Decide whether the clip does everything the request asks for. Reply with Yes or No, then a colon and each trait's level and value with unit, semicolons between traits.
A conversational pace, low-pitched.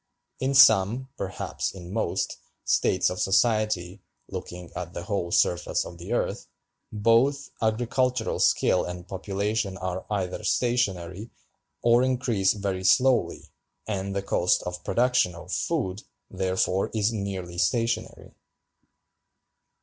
No: slow, 120 wpm; low, 100 Hz